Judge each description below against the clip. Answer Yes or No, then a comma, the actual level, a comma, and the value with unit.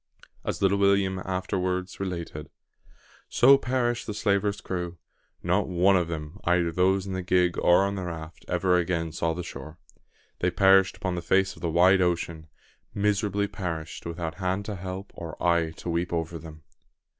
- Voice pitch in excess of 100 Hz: No, very low, 90 Hz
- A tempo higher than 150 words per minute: Yes, average, 170 wpm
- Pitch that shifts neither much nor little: No, narrow, 2.3 semitones